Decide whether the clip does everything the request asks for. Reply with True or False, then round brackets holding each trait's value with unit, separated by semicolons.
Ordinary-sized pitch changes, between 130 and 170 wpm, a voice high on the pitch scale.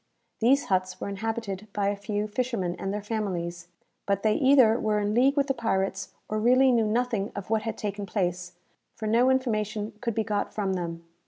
False (3.0 semitones; 195 wpm; 210 Hz)